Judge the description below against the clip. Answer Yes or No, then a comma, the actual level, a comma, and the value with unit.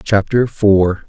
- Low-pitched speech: Yes, low, 105 Hz